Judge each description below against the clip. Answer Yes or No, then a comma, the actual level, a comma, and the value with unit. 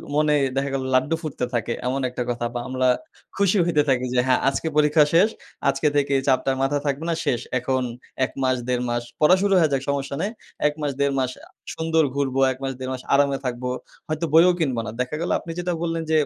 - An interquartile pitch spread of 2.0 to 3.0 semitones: No, average, 3.6 semitones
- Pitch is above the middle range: No, medium, 140 Hz